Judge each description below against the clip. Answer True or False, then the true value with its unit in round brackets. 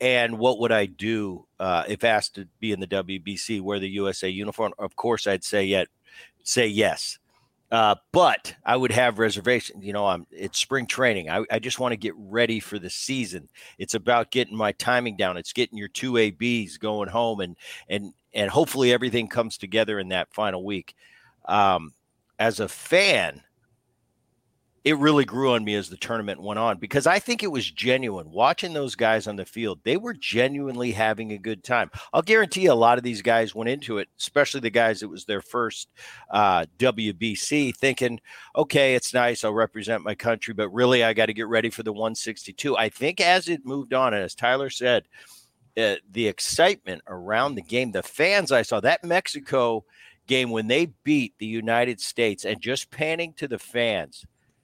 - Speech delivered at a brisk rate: False (195 wpm)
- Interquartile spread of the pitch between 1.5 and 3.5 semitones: True (3.1 semitones)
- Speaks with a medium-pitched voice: False (115 Hz)